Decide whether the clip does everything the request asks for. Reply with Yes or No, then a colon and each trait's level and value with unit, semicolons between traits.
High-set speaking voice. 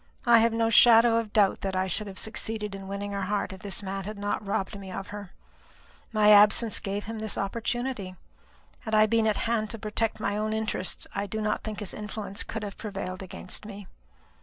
Yes: high, 210 Hz